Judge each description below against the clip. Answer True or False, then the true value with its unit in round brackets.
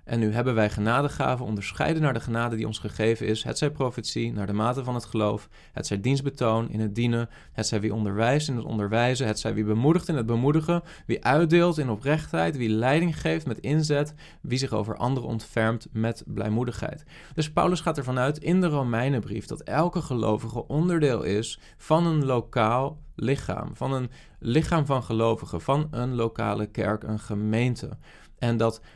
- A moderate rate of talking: True (180 wpm)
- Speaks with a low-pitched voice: True (120 Hz)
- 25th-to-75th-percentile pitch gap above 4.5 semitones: True (4.9 semitones)